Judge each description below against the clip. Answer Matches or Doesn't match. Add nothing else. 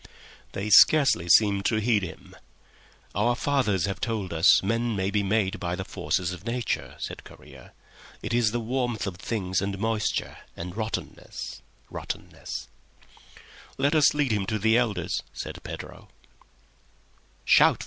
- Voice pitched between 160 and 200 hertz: Doesn't match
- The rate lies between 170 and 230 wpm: Doesn't match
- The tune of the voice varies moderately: Matches